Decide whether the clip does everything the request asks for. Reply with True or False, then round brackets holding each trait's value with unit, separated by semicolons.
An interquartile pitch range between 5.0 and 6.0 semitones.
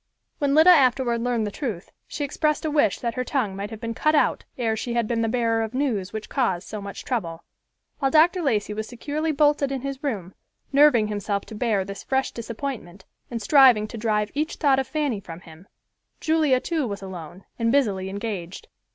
True (5.3 semitones)